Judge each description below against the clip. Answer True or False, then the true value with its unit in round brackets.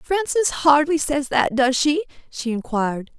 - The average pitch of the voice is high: True (285 Hz)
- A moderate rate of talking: True (150 wpm)